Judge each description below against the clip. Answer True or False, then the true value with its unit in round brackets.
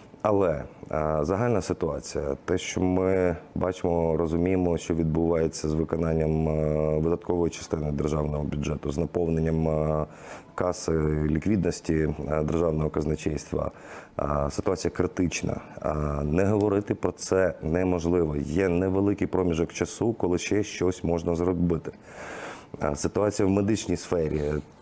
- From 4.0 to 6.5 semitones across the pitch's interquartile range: False (2.8 semitones)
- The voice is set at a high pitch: False (85 Hz)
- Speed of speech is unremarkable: False (100 wpm)